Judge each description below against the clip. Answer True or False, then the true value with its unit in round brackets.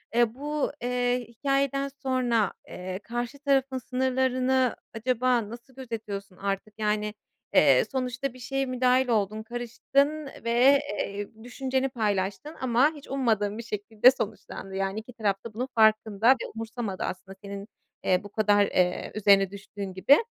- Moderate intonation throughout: True (4.1 semitones)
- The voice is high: True (235 Hz)